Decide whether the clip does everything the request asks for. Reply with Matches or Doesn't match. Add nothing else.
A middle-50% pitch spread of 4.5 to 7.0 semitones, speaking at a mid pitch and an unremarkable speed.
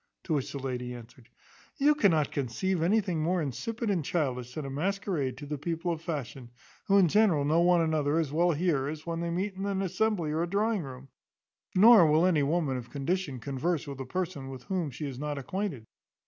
Doesn't match